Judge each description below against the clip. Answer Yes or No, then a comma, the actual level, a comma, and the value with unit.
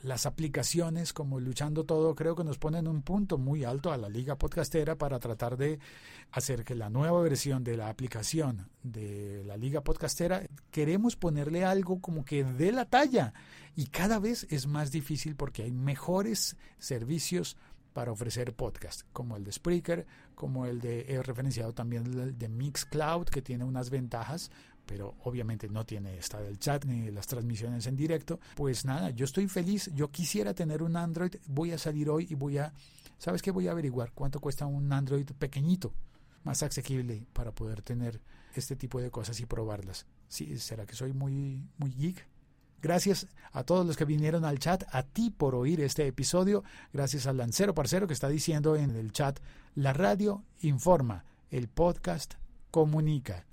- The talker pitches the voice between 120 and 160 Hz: Yes, medium, 140 Hz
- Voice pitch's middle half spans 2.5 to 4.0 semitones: No, average, 4.7 semitones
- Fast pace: No, average, 175 wpm